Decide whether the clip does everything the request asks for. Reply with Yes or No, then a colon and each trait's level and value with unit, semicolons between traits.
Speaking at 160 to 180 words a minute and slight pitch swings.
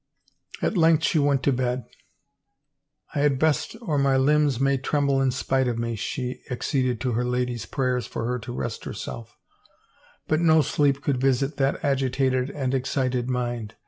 Yes: average, 175 wpm; narrow, 2.2 semitones